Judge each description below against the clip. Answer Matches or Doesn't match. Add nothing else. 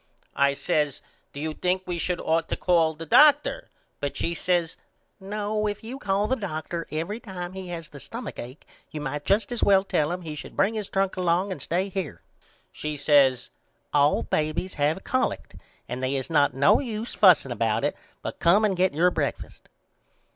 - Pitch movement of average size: Matches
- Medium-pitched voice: Matches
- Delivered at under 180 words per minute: Doesn't match